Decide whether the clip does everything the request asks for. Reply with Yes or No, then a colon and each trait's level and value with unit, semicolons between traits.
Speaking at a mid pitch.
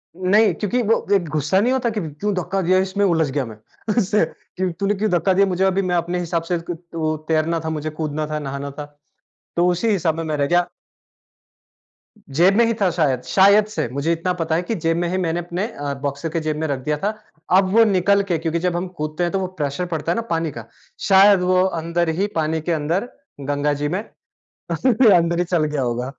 Yes: medium, 170 Hz